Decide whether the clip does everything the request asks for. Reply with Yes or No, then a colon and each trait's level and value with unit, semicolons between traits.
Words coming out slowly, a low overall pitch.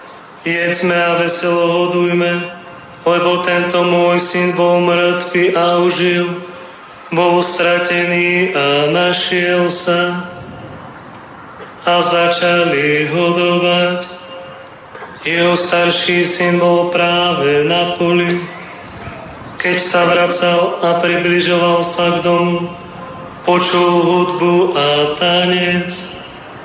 No: slow, 90 wpm; medium, 175 Hz